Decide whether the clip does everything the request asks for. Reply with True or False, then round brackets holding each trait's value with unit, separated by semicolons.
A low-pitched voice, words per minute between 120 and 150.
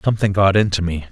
False (95 Hz; 215 wpm)